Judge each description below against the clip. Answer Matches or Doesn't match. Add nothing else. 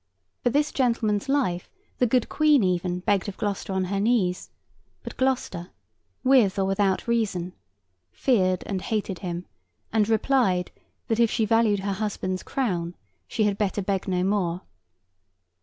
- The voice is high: Matches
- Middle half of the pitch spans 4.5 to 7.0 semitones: Doesn't match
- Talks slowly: Doesn't match